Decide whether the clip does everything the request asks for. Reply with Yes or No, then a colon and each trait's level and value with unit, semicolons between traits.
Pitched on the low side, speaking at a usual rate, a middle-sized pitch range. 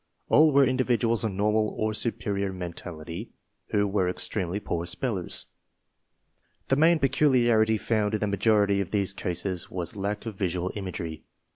Yes: low, 105 Hz; average, 145 wpm; average, 3.5 semitones